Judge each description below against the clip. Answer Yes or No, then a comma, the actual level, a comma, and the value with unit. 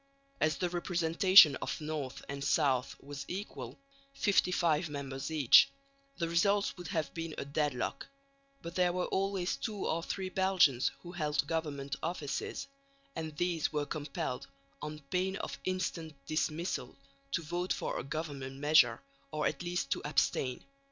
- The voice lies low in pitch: No, medium, 160 Hz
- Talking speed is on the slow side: No, average, 145 wpm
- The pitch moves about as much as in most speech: Yes, average, 3.7 semitones